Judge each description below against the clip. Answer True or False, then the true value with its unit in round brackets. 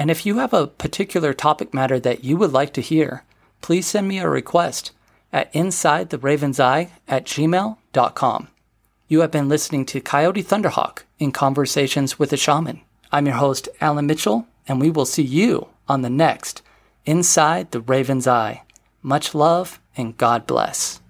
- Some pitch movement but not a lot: True (3.4 semitones)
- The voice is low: False (145 Hz)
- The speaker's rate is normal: True (170 wpm)